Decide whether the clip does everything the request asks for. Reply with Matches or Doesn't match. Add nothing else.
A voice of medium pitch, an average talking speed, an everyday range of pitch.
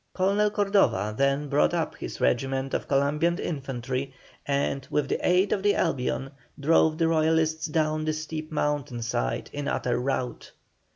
Matches